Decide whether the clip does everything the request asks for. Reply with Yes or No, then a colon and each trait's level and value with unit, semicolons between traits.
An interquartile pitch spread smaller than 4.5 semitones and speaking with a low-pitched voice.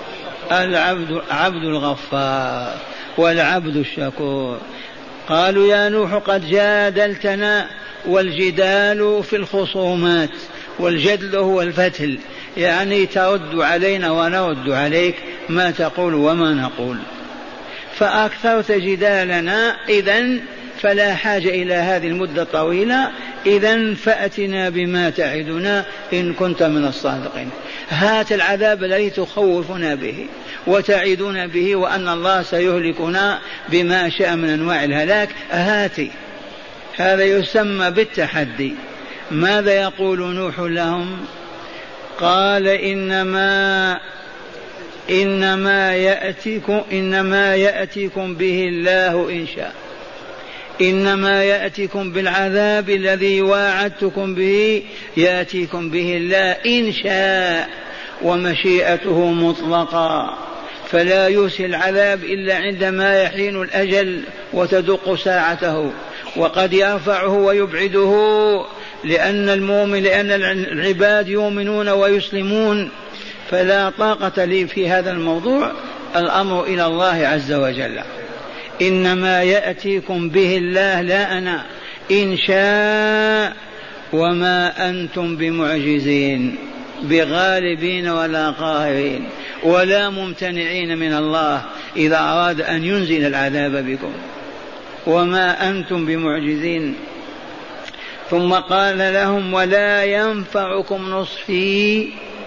No: narrow, 2.6 semitones; high, 190 Hz